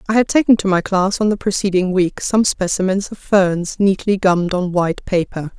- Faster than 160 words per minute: Yes, fast, 205 wpm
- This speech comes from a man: No, female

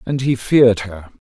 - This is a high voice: No, low, 115 Hz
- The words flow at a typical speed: Yes, average, 190 wpm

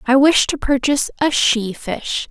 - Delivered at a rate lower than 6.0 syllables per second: Yes, 4.4 syllables/s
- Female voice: Yes, female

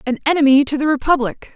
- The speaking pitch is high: Yes, very high, 280 Hz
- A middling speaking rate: Yes, average, 195 wpm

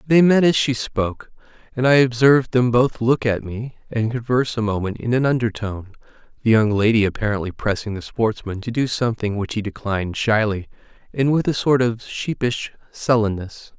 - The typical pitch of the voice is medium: No, low, 115 Hz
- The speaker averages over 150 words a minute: Yes, average, 185 wpm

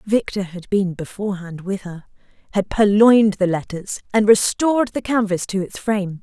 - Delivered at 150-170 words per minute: Yes, average, 165 wpm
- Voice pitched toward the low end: No, high, 200 Hz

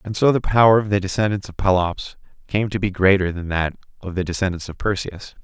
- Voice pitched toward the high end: No, very low, 95 Hz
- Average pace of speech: No, fast, 220 wpm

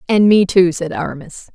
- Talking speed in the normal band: Yes, average, 195 wpm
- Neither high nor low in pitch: Yes, medium, 180 Hz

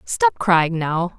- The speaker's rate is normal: Yes, average, 150 wpm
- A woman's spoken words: Yes, female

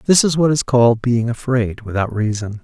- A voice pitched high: No, low, 120 Hz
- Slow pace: No, fast, 205 wpm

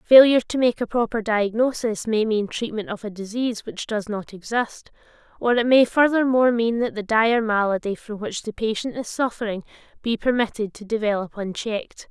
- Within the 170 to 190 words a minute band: Yes, average, 180 wpm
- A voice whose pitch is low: No, high, 220 Hz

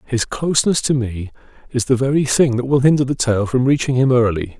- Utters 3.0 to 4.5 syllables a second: No, 5.6 syllables/s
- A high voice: No, low, 125 Hz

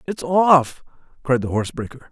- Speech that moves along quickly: No, average, 170 wpm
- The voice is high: No, medium, 145 Hz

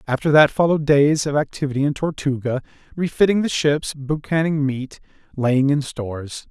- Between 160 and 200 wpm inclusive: No, average, 150 wpm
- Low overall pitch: No, medium, 145 Hz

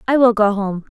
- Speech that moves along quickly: Yes, fast, 250 wpm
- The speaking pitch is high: Yes, high, 220 Hz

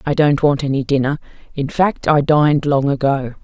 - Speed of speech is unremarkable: Yes, average, 190 wpm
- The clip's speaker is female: Yes, female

